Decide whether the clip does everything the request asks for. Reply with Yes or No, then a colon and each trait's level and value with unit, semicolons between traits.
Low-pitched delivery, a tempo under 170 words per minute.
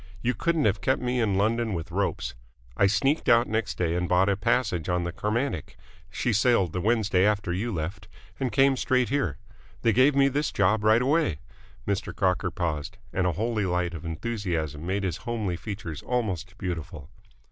No: low, 100 Hz; average, 185 wpm